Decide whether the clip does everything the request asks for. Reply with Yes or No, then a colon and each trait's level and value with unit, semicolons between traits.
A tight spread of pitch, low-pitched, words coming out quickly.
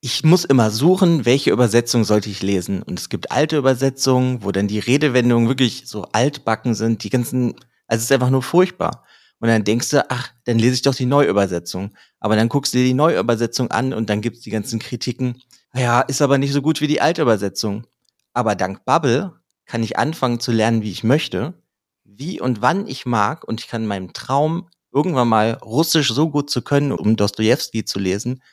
No: average, 3.7 semitones; low, 125 Hz; fast, 205 wpm